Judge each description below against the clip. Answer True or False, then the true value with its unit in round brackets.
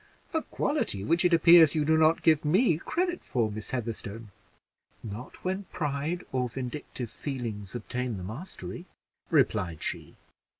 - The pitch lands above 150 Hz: False (140 Hz)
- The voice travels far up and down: True (6.8 semitones)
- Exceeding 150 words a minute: False (140 wpm)